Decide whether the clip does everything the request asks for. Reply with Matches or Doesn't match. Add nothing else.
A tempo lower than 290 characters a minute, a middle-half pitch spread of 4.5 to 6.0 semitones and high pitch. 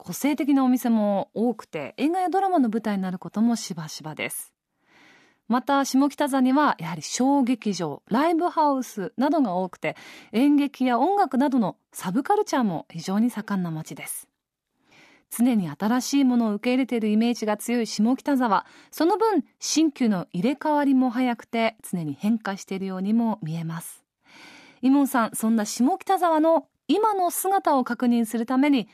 Doesn't match